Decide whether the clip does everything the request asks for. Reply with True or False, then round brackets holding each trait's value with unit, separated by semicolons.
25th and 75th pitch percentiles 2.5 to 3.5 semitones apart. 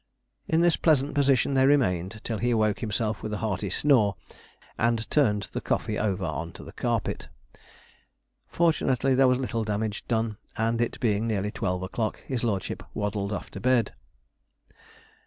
False (3.9 semitones)